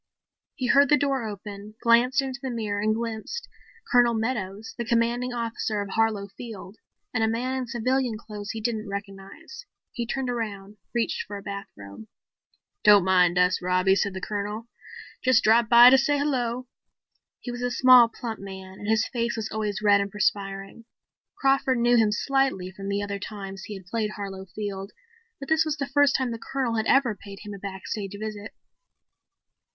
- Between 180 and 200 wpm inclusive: Yes, average, 185 wpm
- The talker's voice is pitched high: Yes, high, 220 Hz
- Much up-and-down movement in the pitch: No, average, 3.6 semitones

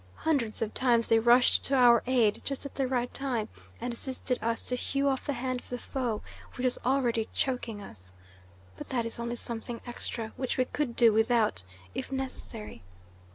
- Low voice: No, high, 245 Hz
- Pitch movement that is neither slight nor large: No, narrow, 2.3 semitones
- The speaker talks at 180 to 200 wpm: Yes, average, 190 wpm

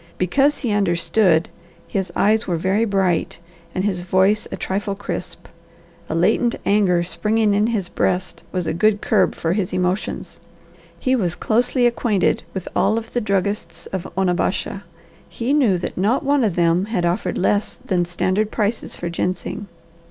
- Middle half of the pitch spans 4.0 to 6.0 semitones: No, average, 3.2 semitones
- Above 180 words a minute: No, average, 165 wpm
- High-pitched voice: Yes, high, 195 Hz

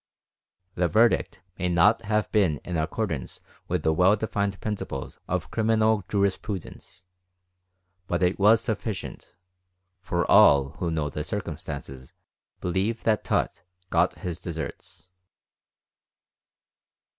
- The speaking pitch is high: No, very low, 95 Hz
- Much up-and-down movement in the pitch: No, average, 3.9 semitones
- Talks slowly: Yes, slow, 110 wpm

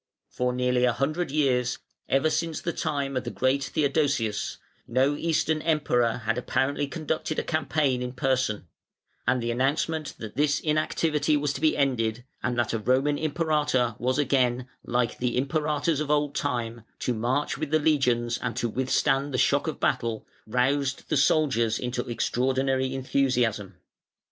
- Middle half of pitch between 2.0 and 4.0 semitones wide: Yes, average, 3.2 semitones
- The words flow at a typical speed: Yes, average, 160 wpm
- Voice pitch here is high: No, low, 135 Hz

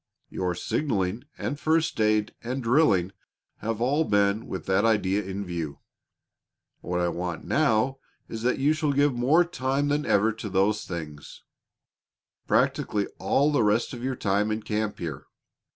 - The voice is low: Yes, low, 110 Hz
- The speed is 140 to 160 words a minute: Yes, average, 155 wpm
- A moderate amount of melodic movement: No, wide, 5.7 semitones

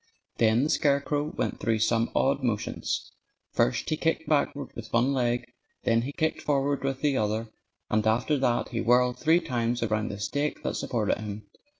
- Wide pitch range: No, average, 4.0 semitones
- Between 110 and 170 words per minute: No, average, 180 wpm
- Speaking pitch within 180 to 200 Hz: No, low, 125 Hz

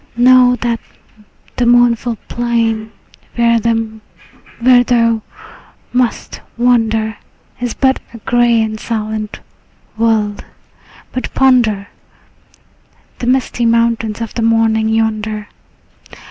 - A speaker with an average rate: No, slow, 90 wpm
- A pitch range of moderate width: No, narrow, 1.6 semitones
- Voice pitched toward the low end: No, high, 230 Hz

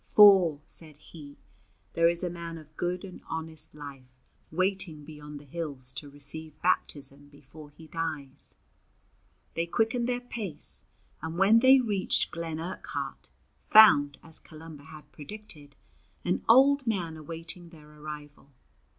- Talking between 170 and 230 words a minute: No, slow, 135 wpm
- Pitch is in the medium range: Yes, medium, 160 Hz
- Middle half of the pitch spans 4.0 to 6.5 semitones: No, average, 3.6 semitones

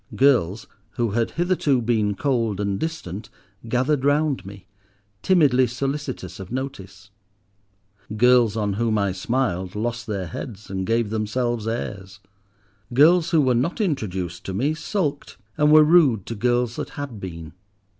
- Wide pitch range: Yes, wide, 5.7 semitones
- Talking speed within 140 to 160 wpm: Yes, average, 145 wpm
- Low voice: Yes, low, 120 Hz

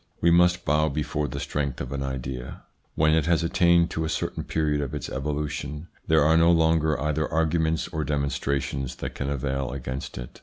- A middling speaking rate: Yes, average, 190 wpm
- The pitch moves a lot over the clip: No, average, 2.7 semitones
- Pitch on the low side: Yes, very low, 75 Hz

